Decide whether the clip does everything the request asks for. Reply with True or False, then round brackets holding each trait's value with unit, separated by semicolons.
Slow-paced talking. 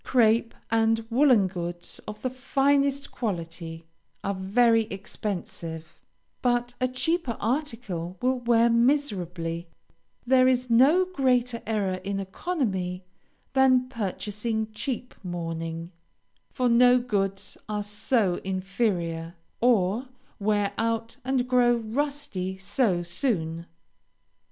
True (105 wpm)